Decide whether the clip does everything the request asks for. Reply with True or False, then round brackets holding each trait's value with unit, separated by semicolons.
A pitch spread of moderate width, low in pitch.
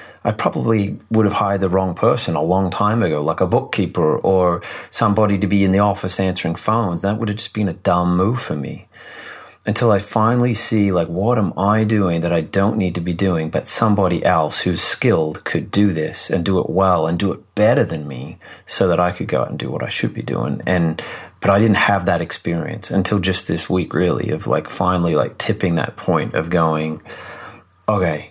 True (3.1 semitones; 95 Hz)